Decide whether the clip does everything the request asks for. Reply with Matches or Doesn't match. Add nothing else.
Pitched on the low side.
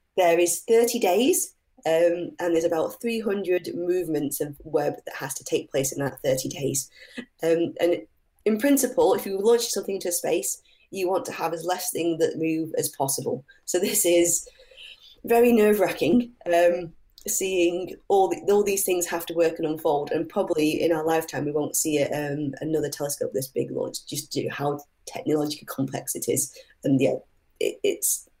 Doesn't match